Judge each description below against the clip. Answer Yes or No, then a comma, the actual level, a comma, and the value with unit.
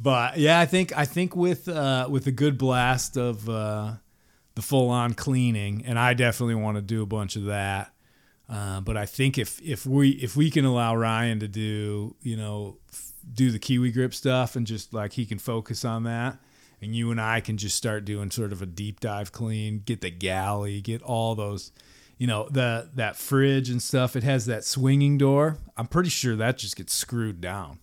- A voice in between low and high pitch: No, low, 115 Hz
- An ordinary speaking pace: No, fast, 210 wpm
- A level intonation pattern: No, average, 3.7 semitones